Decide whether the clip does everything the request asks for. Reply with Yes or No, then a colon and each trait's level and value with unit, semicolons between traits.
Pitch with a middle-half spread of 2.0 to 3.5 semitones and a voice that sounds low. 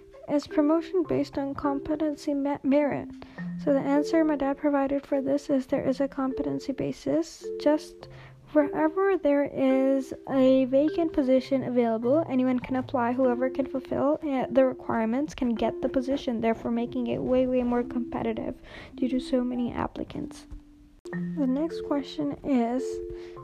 No: narrow, 2.6 semitones; very high, 275 Hz